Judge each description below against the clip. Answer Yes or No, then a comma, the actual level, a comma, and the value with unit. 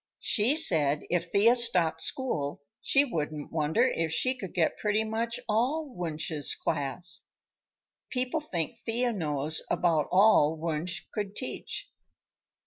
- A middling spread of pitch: No, wide, 7.0 semitones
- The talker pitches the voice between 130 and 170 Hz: No, medium, 180 Hz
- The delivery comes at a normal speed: No, slow, 130 wpm